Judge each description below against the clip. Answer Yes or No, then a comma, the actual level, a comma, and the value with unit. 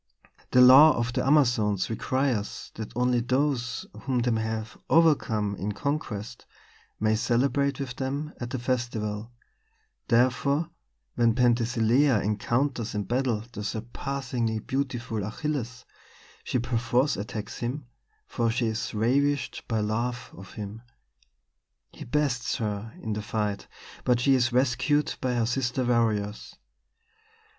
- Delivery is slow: Yes, slow, 125 wpm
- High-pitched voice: No, low, 120 Hz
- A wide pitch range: No, average, 3.1 semitones